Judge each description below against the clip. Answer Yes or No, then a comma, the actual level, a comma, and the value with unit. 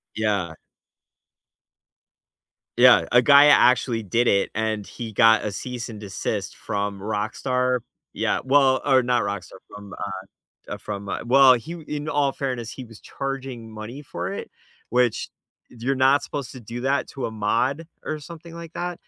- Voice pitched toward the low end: Yes, low, 125 Hz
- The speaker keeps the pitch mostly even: No, average, 4.1 semitones